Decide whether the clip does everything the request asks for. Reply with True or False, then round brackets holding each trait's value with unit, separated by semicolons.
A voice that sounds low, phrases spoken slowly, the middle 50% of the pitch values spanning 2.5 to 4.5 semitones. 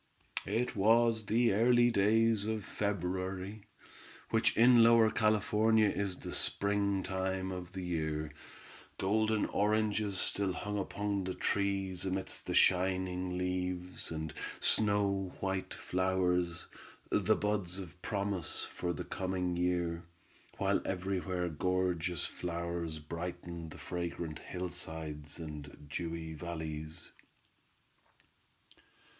True (95 Hz; 105 wpm; 2.8 semitones)